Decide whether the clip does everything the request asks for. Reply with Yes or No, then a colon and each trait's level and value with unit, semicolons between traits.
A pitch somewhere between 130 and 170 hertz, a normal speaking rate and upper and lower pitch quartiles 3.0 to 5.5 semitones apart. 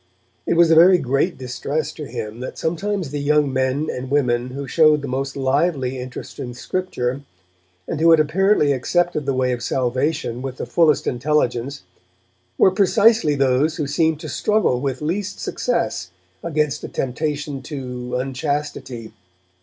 Yes: medium, 140 Hz; average, 155 wpm; average, 3.7 semitones